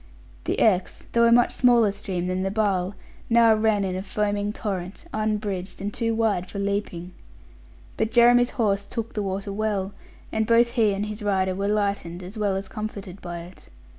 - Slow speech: No, average, 185 wpm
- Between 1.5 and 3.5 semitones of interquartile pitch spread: Yes, narrow, 2.4 semitones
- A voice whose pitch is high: Yes, high, 205 Hz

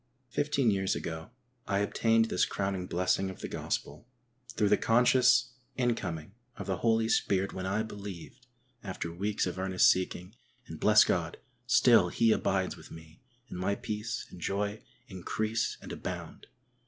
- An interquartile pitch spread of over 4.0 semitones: No, average, 3.4 semitones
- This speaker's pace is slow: No, average, 155 wpm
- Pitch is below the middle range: Yes, low, 100 Hz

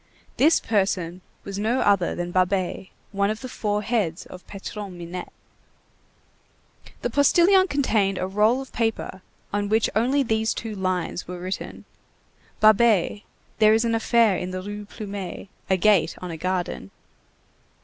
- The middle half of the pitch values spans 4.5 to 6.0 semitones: No, average, 3.3 semitones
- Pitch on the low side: No, high, 205 Hz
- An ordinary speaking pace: Yes, average, 150 wpm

